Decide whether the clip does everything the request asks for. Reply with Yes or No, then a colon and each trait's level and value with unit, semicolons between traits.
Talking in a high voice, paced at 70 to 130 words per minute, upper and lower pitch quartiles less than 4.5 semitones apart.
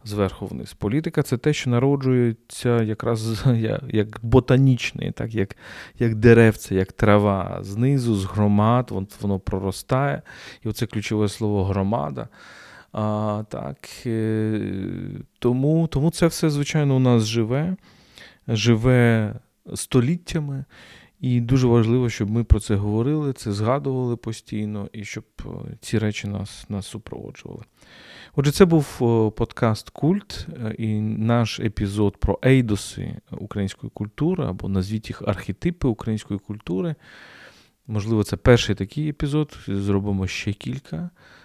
No: low, 115 Hz; average, 120 wpm; average, 3.8 semitones